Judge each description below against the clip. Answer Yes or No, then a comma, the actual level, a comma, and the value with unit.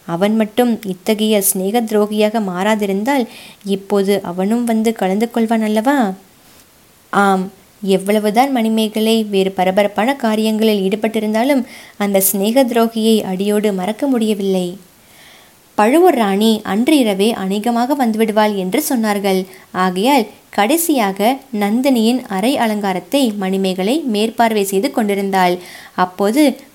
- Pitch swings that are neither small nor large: Yes, average, 3.2 semitones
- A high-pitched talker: Yes, high, 215 Hz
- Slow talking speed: No, average, 95 wpm